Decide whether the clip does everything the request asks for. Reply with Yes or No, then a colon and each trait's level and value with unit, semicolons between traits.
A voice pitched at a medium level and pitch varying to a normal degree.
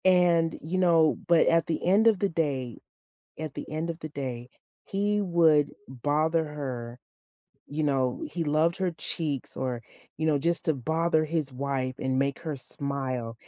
Yes: medium, 155 Hz; average, 3.8 semitones